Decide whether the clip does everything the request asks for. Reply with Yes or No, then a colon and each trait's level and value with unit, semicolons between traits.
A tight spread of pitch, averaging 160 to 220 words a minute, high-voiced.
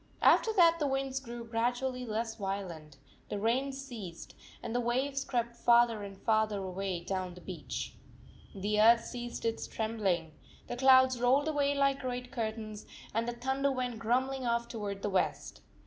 No: average, 3.9 semitones; average, 165 wpm; high, 235 Hz